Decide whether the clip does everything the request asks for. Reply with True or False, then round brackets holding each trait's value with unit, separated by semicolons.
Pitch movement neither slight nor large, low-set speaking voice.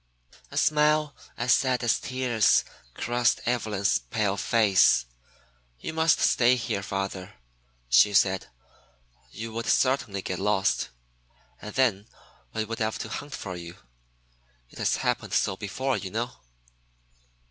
True (4.5 semitones; 110 Hz)